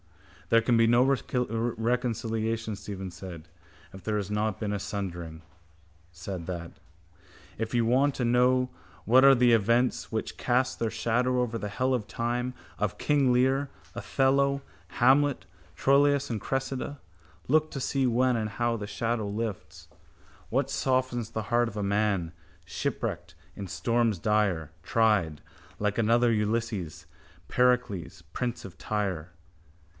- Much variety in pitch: No, average, 3.4 semitones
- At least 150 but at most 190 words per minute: No, average, 140 wpm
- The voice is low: Yes, low, 115 Hz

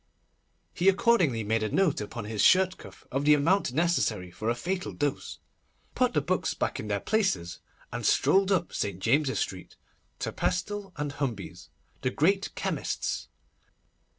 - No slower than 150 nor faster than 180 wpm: Yes, average, 155 wpm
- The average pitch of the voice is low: No, medium, 145 Hz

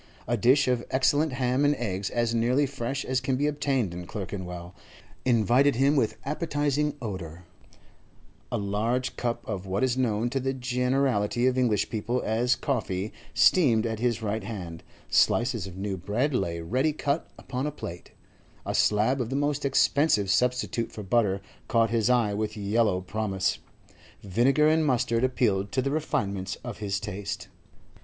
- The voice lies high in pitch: No, low, 120 Hz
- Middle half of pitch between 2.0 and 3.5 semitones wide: No, average, 4.5 semitones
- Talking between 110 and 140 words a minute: No, average, 165 wpm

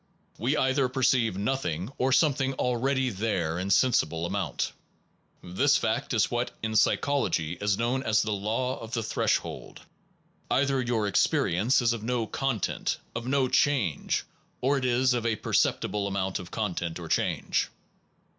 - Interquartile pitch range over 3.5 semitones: Yes, average, 4.8 semitones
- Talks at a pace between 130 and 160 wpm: Yes, average, 150 wpm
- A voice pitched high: No, low, 115 Hz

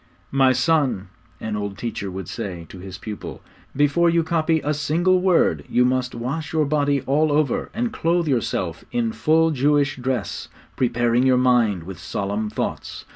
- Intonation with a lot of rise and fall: Yes, wide, 6.5 semitones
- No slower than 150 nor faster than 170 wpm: Yes, average, 165 wpm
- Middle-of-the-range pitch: No, low, 130 Hz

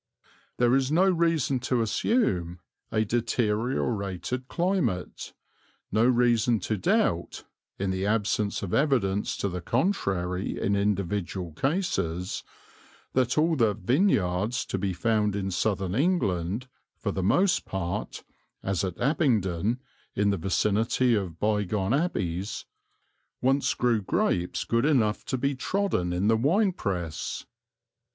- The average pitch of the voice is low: Yes, low, 110 Hz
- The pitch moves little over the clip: No, wide, 5.4 semitones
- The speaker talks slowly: Yes, slow, 125 wpm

